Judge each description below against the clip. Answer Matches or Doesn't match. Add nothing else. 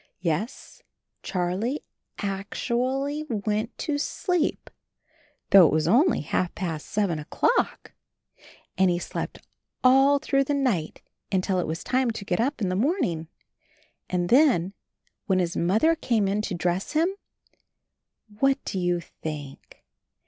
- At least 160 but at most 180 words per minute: Doesn't match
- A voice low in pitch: Doesn't match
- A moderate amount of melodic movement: Doesn't match